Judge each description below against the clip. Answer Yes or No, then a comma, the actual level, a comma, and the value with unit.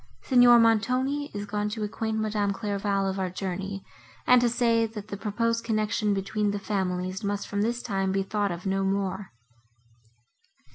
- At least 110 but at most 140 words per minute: No, average, 165 wpm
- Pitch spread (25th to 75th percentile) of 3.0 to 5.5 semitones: No, narrow, 2.6 semitones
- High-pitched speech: Yes, high, 205 Hz